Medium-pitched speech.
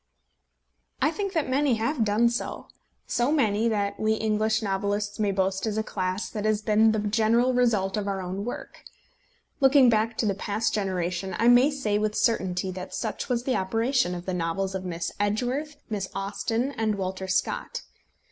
No: high, 215 Hz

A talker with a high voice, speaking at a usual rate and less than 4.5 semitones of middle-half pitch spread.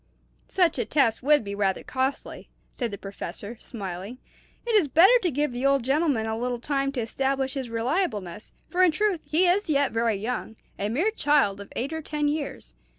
No: very high, 265 Hz; average, 195 wpm; average, 5.2 semitones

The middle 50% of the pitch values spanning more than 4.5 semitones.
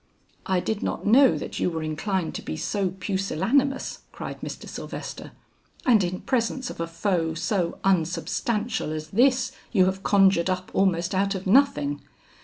No: average, 4.2 semitones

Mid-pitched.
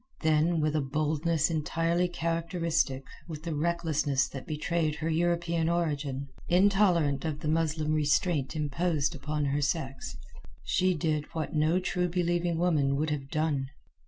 Yes: medium, 155 Hz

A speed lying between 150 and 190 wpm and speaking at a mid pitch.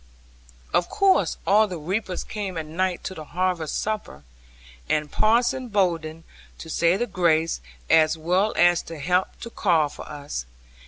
Yes: average, 155 wpm; medium, 175 Hz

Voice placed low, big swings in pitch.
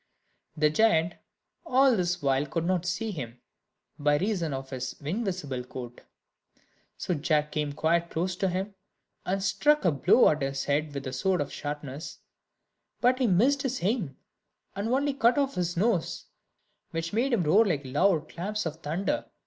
No: medium, 170 Hz; wide, 6.0 semitones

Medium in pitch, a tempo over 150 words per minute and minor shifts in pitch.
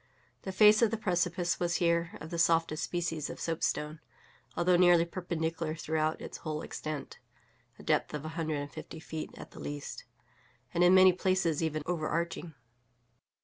Yes: medium, 165 Hz; average, 165 wpm; narrow, 2.1 semitones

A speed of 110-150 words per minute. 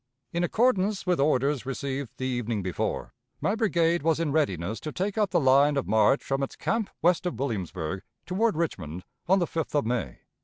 No: average, 190 wpm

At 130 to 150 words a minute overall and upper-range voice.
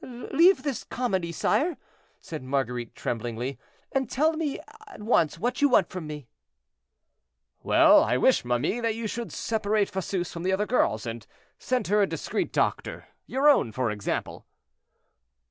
No: average, 160 wpm; high, 195 Hz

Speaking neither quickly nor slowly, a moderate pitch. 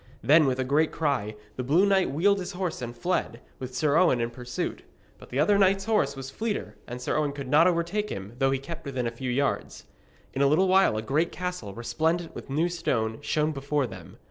No: fast, 220 wpm; medium, 145 Hz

